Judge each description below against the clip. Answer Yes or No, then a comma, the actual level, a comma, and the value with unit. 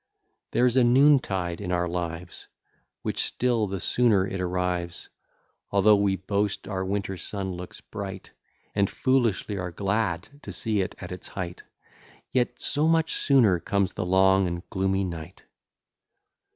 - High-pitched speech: No, very low, 95 Hz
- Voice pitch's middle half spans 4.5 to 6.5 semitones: No, average, 3.0 semitones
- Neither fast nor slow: Yes, average, 150 wpm